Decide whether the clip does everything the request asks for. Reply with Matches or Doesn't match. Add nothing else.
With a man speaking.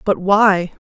Doesn't match